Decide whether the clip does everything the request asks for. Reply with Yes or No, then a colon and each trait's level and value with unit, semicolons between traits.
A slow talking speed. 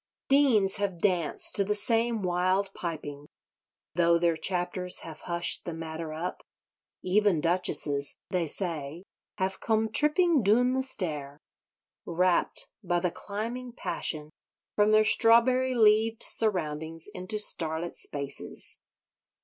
Yes: slow, 120 wpm